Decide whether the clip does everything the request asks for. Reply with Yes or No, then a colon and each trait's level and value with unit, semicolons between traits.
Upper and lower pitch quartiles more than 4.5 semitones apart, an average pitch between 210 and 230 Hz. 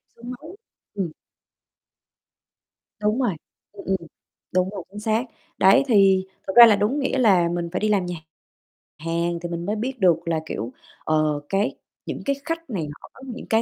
No: average, 5.1 semitones; high, 195 Hz